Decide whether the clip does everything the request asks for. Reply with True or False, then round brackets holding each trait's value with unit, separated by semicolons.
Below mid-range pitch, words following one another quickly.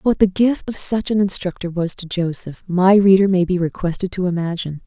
False (185 Hz; 210 wpm)